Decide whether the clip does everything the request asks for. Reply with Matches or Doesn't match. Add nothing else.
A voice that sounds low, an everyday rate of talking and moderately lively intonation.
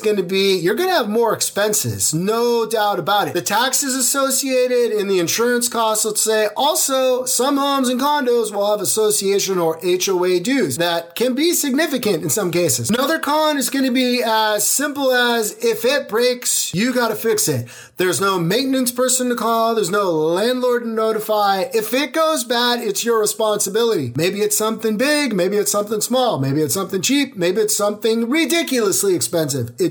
Doesn't match